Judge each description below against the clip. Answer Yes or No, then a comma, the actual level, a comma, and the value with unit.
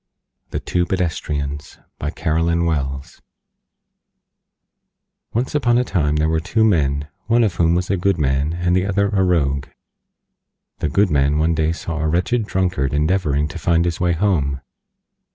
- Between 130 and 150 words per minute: No, average, 160 wpm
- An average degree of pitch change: Yes, average, 4.0 semitones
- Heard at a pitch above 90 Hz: No, very low, 85 Hz